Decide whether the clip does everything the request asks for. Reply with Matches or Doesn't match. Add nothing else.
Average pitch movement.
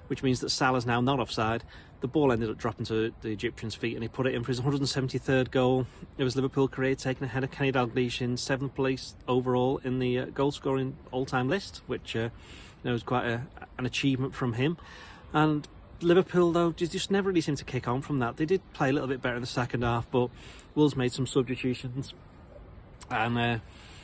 Doesn't match